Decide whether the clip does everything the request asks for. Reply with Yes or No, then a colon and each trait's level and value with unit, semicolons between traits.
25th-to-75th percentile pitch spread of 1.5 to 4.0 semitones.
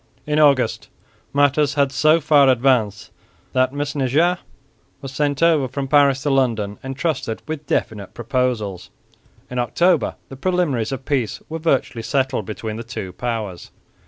Yes: average, 3.6 semitones